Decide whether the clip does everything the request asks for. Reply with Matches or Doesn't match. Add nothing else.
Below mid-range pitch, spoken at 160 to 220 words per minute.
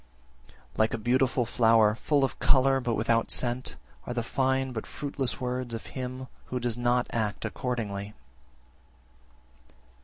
Doesn't match